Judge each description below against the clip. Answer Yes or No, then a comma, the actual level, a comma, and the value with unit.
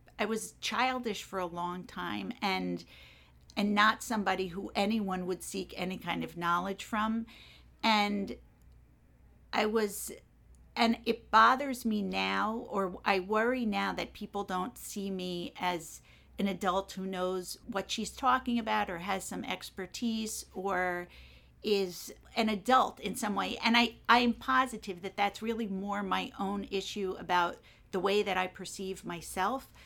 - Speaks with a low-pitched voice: No, high, 200 Hz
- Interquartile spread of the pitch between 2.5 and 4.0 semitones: Yes, average, 3.1 semitones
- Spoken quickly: No, average, 155 wpm